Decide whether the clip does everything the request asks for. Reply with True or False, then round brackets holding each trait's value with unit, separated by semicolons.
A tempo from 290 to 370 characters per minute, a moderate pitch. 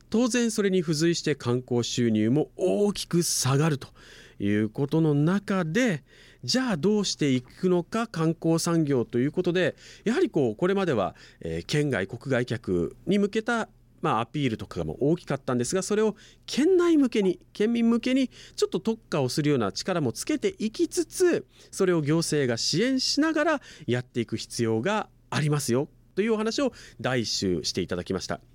True (340 characters per minute; 165 Hz)